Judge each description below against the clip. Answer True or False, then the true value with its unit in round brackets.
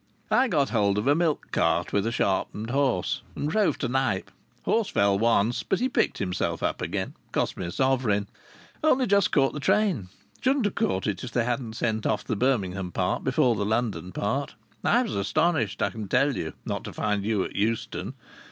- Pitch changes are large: True (6.0 semitones)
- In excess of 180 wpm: True (200 wpm)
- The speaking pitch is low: True (115 Hz)